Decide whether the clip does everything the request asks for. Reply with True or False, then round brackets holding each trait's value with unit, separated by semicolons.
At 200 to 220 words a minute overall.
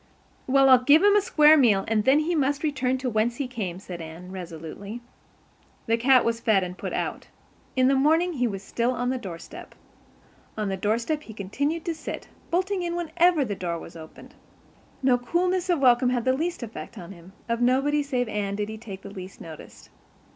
True (205 wpm)